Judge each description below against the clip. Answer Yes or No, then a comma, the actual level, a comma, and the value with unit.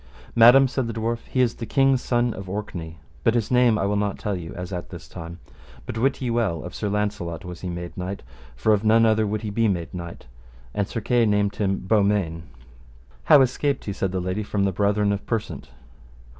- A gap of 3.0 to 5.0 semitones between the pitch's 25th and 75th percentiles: Yes, average, 3.8 semitones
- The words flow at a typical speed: No, fast, 220 wpm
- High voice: No, low, 105 Hz